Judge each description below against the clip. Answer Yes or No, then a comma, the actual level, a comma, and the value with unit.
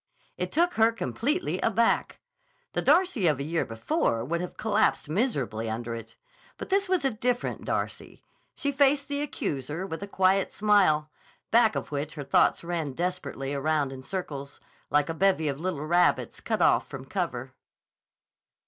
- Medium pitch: Yes, medium, 175 Hz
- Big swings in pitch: Yes, wide, 8.0 semitones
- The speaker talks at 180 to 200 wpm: No, average, 165 wpm